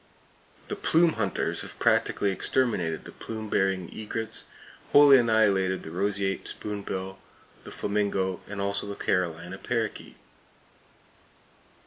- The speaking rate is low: Yes, slow, 110 wpm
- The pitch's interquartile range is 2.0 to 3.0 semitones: Yes, narrow, 2.6 semitones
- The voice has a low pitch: Yes, low, 100 Hz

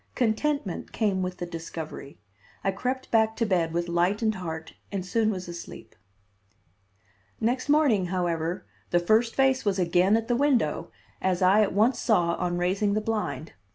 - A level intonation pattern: No, average, 4.3 semitones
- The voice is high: Yes, high, 195 Hz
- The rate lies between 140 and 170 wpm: Yes, average, 160 wpm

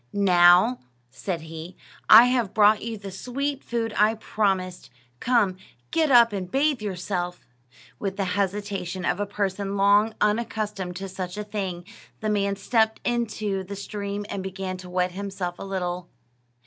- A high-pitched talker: Yes, high, 200 Hz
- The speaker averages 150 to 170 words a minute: Yes, average, 155 wpm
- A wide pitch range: No, average, 2.8 semitones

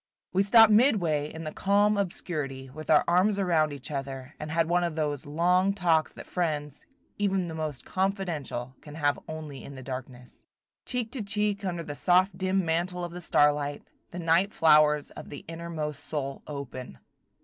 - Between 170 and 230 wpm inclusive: Yes, average, 175 wpm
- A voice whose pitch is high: No, medium, 160 Hz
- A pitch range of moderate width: Yes, average, 4.2 semitones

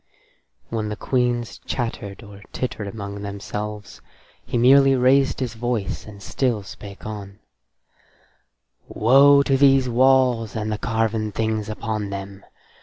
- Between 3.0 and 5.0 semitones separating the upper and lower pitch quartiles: Yes, average, 3.6 semitones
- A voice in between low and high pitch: No, low, 110 Hz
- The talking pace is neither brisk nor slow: No, slow, 125 wpm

